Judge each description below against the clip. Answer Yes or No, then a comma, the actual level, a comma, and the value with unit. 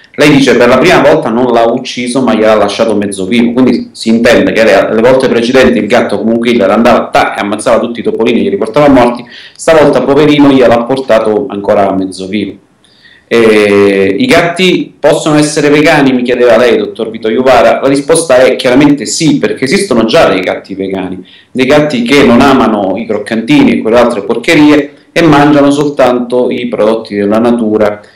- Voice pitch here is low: Yes, low, 125 Hz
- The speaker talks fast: Yes, fast, 180 wpm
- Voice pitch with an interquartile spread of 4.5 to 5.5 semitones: Yes, average, 5.2 semitones